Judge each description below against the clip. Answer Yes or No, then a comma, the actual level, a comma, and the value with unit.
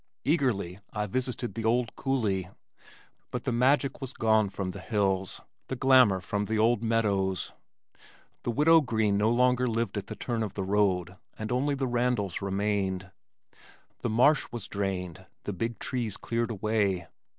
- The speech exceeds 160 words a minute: No, average, 155 wpm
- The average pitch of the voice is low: Yes, low, 110 Hz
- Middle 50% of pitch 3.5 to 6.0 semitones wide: Yes, average, 4.0 semitones